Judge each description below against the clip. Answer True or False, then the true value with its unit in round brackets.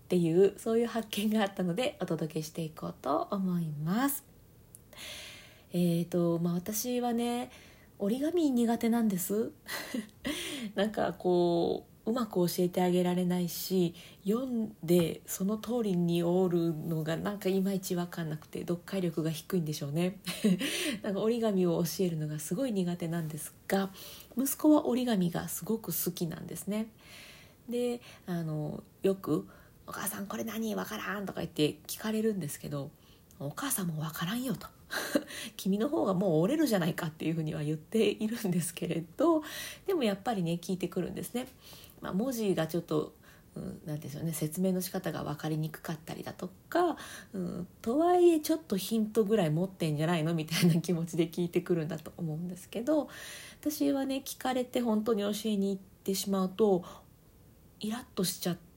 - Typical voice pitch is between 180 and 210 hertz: True (185 Hz)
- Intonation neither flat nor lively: True (4.7 semitones)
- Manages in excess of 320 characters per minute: True (345 characters per minute)